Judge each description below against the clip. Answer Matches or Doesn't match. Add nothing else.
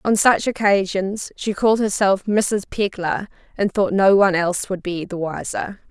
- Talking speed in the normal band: Matches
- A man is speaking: Doesn't match